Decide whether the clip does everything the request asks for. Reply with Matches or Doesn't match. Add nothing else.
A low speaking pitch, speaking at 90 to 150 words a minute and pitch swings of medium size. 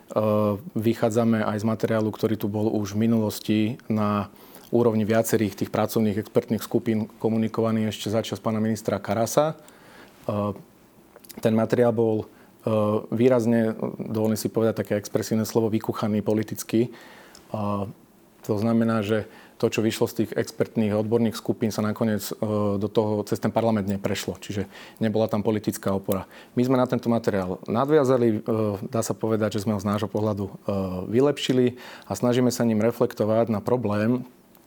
Doesn't match